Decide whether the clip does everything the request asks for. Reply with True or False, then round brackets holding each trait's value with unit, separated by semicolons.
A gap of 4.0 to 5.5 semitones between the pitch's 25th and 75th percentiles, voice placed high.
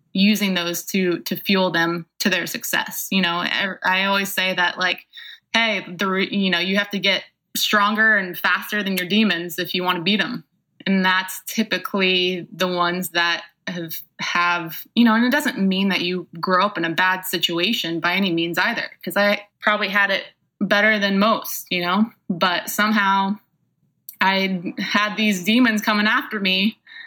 False (2.7 semitones; 195 Hz)